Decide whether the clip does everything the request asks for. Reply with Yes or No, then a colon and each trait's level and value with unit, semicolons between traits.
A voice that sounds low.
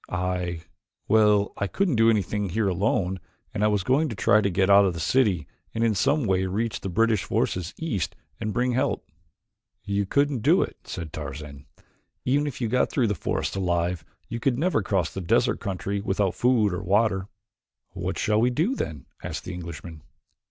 Yes: low, 100 Hz